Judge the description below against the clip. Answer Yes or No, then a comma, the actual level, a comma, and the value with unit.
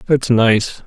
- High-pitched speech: No, low, 115 Hz